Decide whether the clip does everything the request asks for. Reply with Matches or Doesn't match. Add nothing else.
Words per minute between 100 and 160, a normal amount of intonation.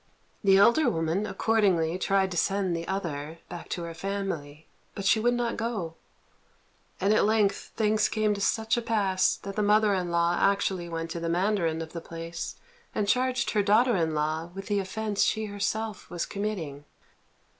Doesn't match